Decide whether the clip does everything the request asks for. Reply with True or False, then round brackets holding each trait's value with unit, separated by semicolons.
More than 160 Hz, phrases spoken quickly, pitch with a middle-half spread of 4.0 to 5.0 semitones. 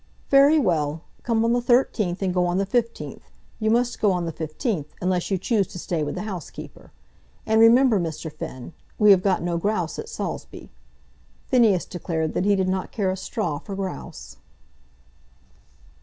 False (190 Hz; 175 wpm; 4.6 semitones)